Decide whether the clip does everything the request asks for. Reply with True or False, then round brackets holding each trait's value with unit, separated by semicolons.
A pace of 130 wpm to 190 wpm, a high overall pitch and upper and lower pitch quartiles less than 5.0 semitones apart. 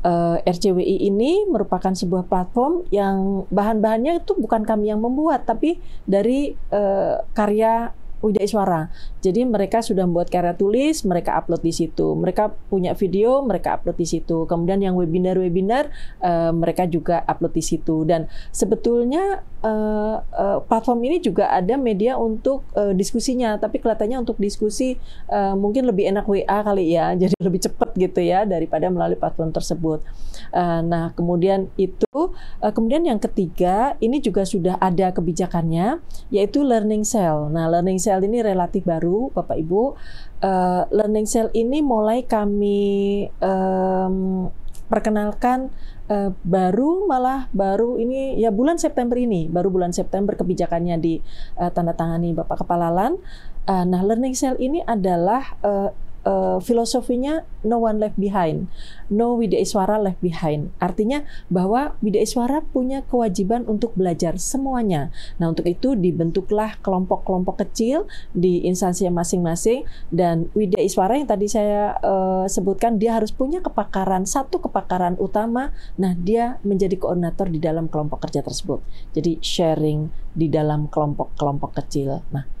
True (140 wpm; 200 Hz; 4.6 semitones)